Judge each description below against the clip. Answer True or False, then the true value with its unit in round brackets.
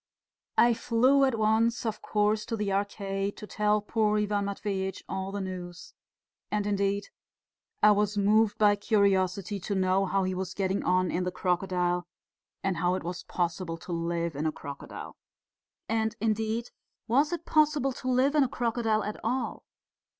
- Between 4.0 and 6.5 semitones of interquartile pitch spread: False (3.0 semitones)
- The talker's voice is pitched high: True (205 Hz)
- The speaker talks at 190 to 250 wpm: False (165 wpm)